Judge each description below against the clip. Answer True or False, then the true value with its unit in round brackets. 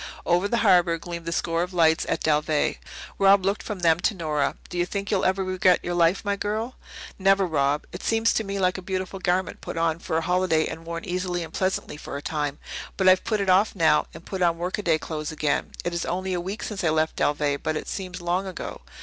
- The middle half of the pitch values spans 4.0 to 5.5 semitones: False (2.7 semitones)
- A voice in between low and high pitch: True (180 Hz)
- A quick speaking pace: True (240 wpm)